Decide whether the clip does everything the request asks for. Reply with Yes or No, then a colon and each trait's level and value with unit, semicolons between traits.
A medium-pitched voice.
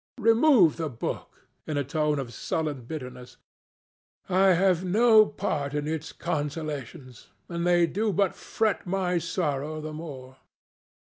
Yes: medium, 160 Hz